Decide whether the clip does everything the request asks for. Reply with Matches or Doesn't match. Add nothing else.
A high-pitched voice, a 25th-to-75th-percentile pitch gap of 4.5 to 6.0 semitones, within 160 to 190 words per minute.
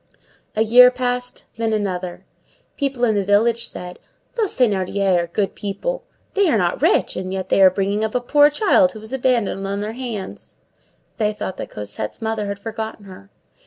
Doesn't match